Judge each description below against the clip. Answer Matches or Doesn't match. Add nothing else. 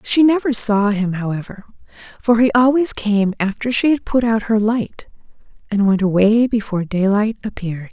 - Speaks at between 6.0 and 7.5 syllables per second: Doesn't match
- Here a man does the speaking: Doesn't match